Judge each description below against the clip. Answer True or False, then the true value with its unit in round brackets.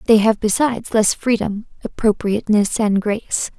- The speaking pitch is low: False (220 Hz)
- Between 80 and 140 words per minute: True (135 wpm)